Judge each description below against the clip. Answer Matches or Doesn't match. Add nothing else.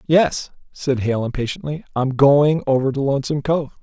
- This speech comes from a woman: Doesn't match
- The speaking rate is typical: Matches